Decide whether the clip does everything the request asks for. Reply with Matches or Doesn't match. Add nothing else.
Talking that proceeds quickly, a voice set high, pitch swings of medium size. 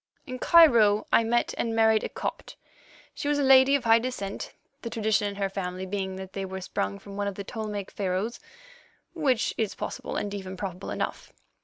Doesn't match